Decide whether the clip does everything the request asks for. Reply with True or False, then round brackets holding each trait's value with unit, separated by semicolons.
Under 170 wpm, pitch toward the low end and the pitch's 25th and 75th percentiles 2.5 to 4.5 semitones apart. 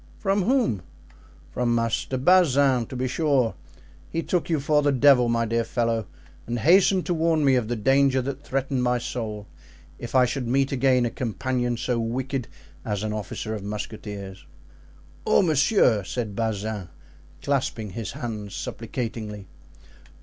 True (150 wpm; 125 Hz; 3.7 semitones)